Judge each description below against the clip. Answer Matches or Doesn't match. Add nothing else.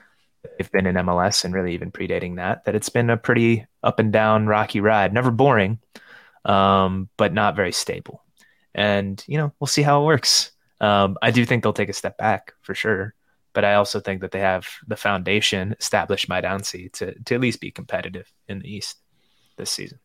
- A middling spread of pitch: Matches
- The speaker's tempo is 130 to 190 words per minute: Doesn't match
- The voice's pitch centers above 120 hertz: Doesn't match